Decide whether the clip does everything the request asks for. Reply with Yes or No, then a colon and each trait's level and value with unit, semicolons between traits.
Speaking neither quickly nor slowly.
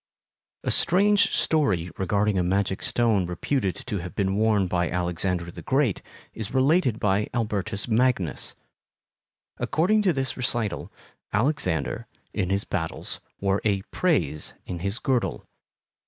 No: slow, 130 wpm